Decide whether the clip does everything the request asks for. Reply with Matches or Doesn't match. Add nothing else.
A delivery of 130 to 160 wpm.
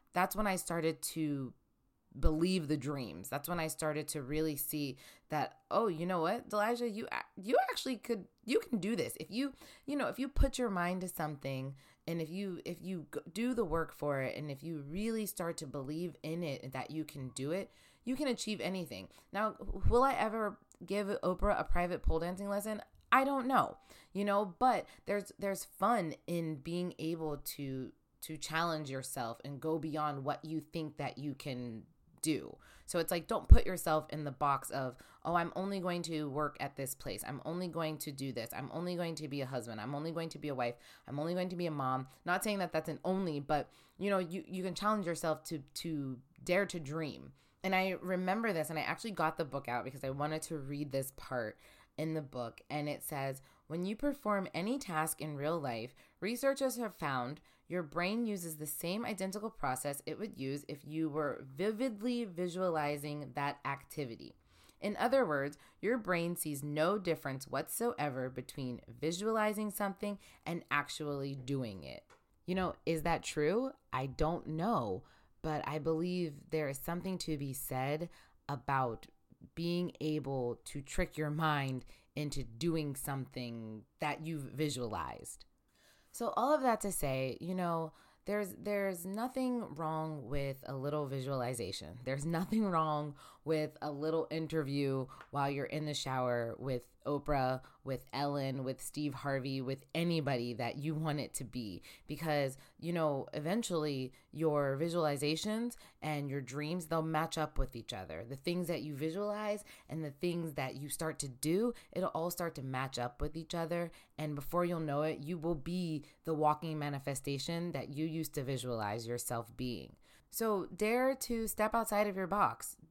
Doesn't match